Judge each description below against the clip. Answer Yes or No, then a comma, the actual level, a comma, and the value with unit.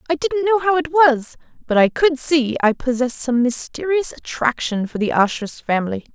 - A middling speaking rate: Yes, average, 185 wpm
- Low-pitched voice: No, very high, 275 Hz